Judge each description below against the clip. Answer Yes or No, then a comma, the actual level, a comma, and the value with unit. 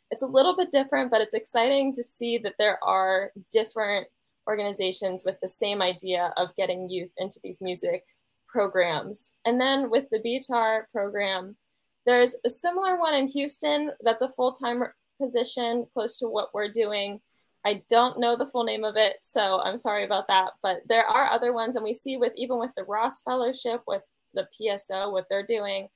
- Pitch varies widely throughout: No, average, 3.8 semitones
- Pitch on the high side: Yes, high, 225 Hz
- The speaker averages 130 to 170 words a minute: No, average, 185 wpm